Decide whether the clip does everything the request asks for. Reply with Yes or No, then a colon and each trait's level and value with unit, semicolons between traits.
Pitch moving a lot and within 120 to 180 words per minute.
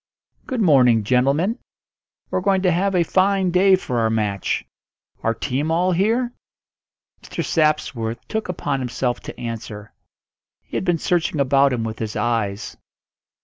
Yes: wide, 8.0 semitones; average, 145 wpm